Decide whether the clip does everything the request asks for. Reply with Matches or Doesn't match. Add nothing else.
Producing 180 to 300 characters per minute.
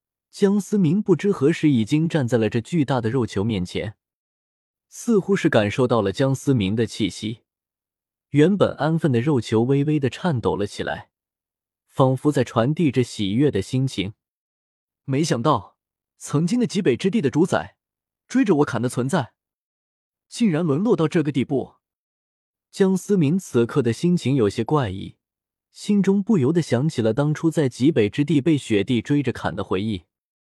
Matches